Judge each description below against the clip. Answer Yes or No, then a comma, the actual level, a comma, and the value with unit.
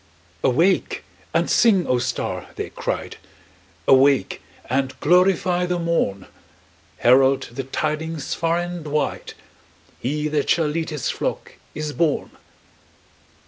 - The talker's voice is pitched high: No, medium, 150 Hz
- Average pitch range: Yes, average, 4.2 semitones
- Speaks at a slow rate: Yes, slow, 115 wpm